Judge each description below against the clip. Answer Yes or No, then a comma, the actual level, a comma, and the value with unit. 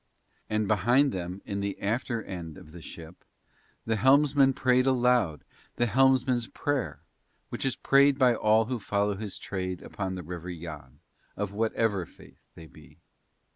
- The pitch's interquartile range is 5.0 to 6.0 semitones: Yes, wide, 5.6 semitones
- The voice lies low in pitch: Yes, low, 110 Hz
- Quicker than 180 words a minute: No, average, 155 wpm